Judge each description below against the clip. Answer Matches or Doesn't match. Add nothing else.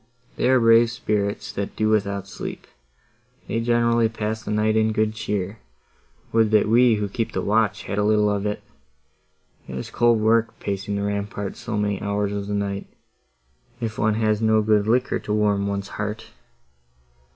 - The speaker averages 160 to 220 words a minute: Matches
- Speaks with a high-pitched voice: Doesn't match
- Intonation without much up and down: Matches